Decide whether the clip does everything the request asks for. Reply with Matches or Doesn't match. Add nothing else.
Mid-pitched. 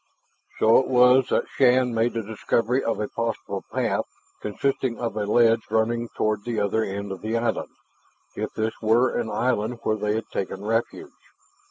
Doesn't match